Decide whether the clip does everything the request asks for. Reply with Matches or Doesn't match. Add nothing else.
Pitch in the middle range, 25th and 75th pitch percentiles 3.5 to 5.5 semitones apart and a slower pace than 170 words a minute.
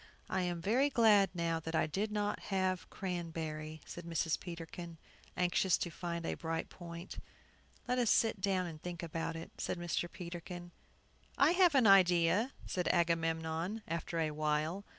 Doesn't match